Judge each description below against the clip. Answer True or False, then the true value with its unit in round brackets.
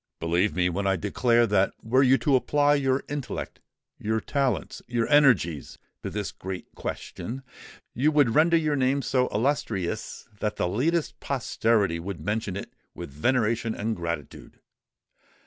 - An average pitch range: False (5.8 semitones)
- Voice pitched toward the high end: False (115 Hz)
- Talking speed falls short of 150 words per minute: True (140 wpm)